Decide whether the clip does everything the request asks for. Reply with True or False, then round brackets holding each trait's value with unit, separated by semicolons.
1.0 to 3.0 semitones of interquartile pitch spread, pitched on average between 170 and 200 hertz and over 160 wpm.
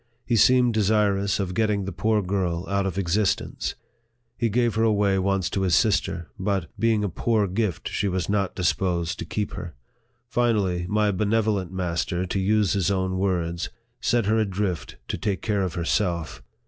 False (2.7 semitones; 100 Hz; 180 wpm)